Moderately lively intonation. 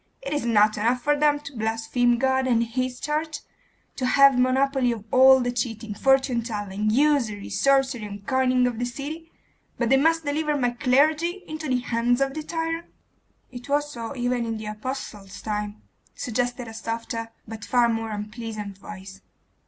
Yes: average, 3.6 semitones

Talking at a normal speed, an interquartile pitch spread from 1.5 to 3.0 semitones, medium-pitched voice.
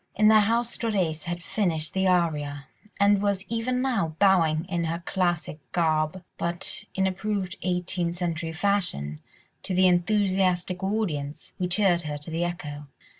No: average, 150 wpm; average, 3.4 semitones; medium, 180 Hz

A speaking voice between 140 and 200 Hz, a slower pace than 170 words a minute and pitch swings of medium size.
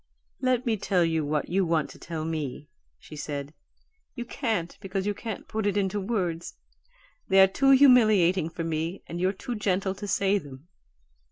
No: high, 190 Hz; average, 180 wpm; average, 4.2 semitones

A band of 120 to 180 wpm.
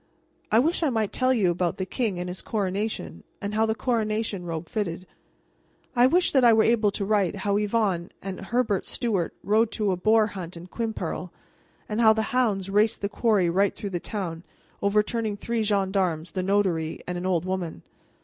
No: average, 190 wpm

